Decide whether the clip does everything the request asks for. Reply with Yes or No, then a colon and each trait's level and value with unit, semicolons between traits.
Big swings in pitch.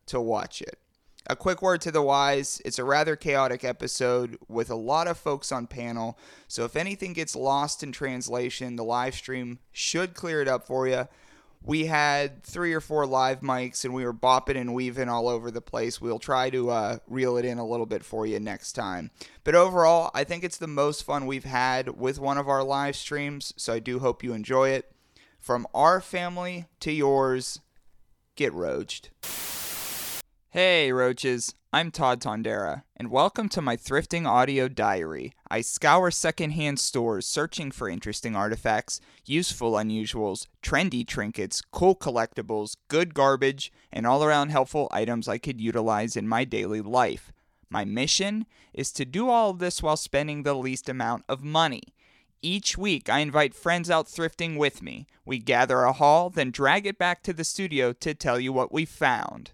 No: average, 4.2 semitones